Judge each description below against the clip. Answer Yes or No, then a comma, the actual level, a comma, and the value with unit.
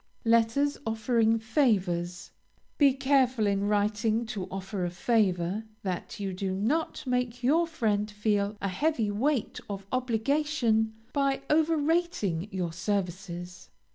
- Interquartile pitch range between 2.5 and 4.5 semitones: No, average, 4.9 semitones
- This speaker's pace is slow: Yes, slow, 125 wpm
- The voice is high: Yes, high, 220 Hz